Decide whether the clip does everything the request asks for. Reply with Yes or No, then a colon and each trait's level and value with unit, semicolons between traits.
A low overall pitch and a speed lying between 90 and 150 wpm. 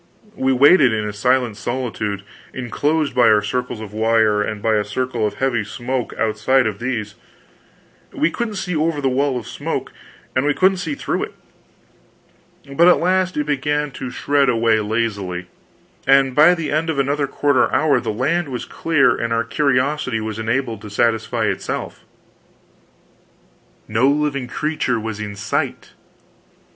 No: low, 125 Hz; average, 160 wpm